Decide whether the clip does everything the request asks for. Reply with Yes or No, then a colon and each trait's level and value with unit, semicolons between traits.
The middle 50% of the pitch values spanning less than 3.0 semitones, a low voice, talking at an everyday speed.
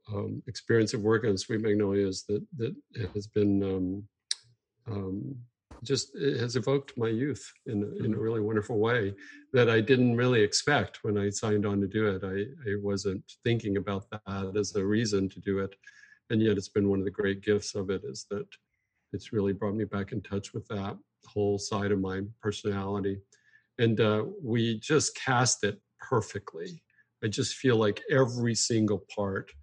Yes: narrow, 2.6 semitones; low, 105 Hz; average, 180 wpm